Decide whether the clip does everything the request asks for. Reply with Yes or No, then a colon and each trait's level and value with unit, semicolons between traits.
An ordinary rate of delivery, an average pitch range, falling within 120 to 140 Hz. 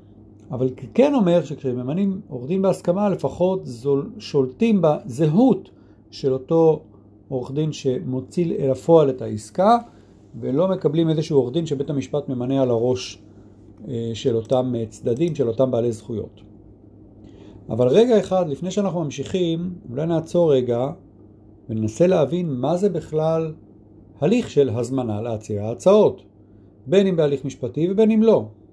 No: average, 130 wpm; wide, 7.6 semitones; low, 135 Hz